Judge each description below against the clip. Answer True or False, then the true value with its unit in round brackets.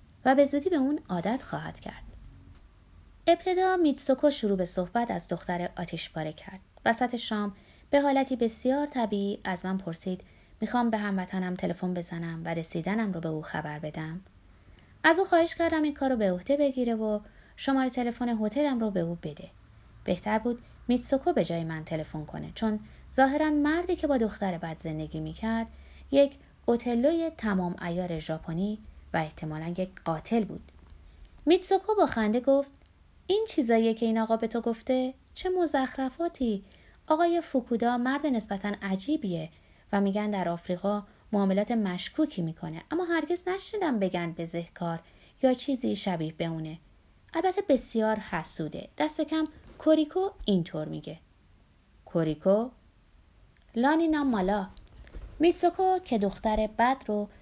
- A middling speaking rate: True (140 wpm)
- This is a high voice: True (220 Hz)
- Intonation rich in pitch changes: True (7.9 semitones)